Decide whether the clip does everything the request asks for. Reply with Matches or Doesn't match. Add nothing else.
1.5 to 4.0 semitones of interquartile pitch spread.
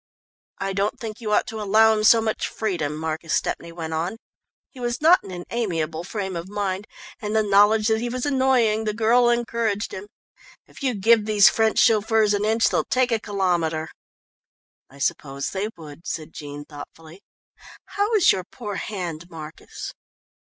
Doesn't match